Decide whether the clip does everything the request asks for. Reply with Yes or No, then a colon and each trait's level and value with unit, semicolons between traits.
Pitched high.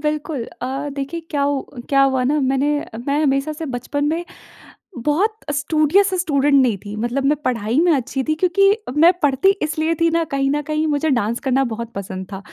Yes: very high, 285 Hz